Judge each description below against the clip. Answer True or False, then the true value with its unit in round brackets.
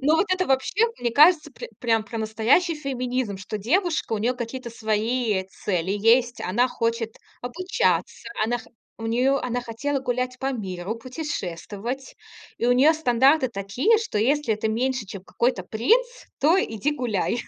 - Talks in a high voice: True (245 Hz)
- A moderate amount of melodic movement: True (3.9 semitones)